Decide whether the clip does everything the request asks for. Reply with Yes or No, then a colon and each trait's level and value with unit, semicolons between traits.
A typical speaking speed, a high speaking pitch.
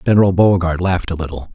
No: average, 195 wpm; very low, 90 Hz